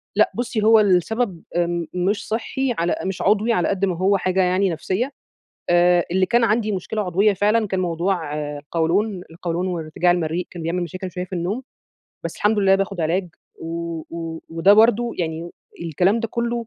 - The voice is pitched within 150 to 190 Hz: Yes, medium, 185 Hz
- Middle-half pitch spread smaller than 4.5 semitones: Yes, average, 3.7 semitones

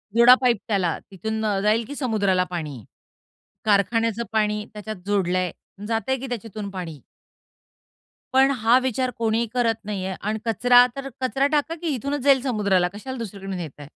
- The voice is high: Yes, high, 220 Hz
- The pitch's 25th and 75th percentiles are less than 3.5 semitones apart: No, average, 4.2 semitones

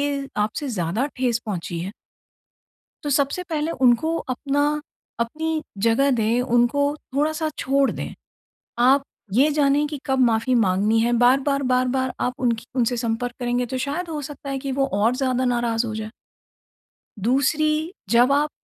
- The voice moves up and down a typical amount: Yes, average, 3.4 semitones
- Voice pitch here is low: No, very high, 255 Hz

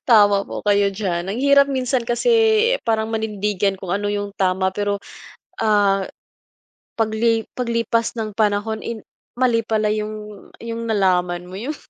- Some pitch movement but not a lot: No, narrow, 2.3 semitones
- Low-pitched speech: No, high, 215 Hz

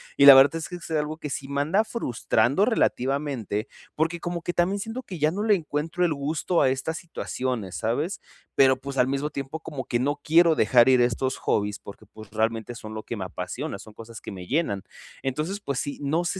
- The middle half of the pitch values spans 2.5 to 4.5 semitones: No, average, 5.2 semitones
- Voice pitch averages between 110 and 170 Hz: Yes, medium, 140 Hz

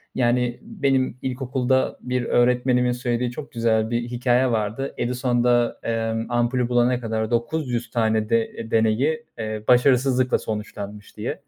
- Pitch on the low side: Yes, low, 120 Hz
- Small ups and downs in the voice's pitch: Yes, narrow, 1.8 semitones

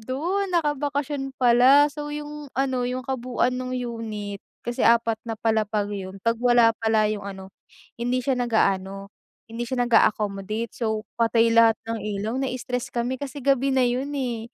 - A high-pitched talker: Yes, high, 240 Hz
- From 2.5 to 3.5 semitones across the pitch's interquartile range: Yes, average, 3.1 semitones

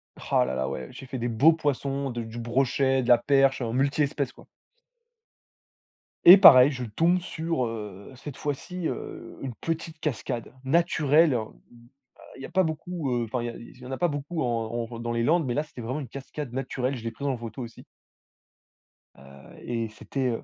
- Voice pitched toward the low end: Yes, low, 130 Hz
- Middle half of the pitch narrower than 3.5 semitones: No, average, 4.2 semitones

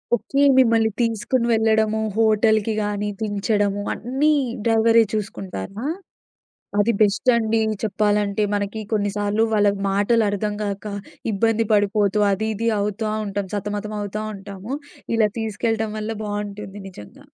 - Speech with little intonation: Yes, narrow, 1.5 semitones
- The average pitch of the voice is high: Yes, high, 210 Hz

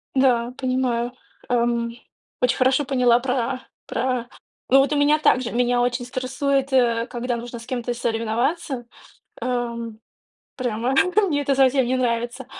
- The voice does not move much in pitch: Yes, narrow, 1.9 semitones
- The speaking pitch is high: Yes, high, 245 Hz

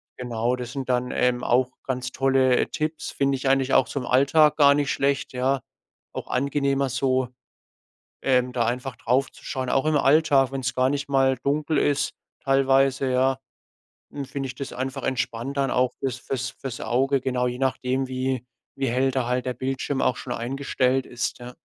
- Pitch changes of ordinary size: No, narrow, 1.5 semitones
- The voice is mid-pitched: No, low, 130 Hz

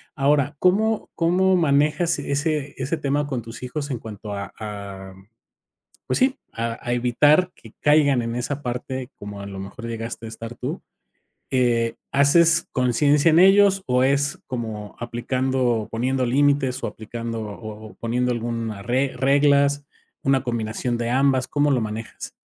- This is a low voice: Yes, low, 130 Hz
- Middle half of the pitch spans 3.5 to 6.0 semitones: Yes, average, 3.8 semitones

